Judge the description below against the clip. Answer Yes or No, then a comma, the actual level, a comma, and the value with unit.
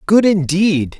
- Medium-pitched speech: Yes, medium, 180 Hz